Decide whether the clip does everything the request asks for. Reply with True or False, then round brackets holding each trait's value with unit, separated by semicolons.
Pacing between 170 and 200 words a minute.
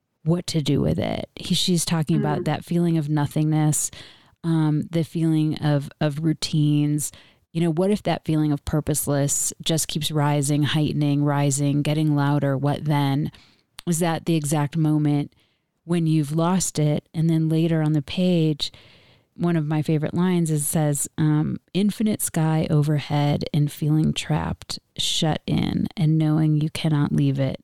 False (160 wpm)